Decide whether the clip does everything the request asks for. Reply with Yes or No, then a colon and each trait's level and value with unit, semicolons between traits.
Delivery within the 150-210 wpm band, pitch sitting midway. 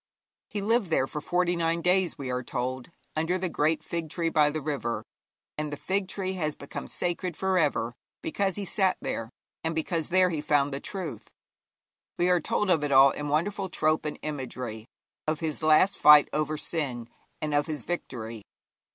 Yes: average, 185 wpm; medium, 155 Hz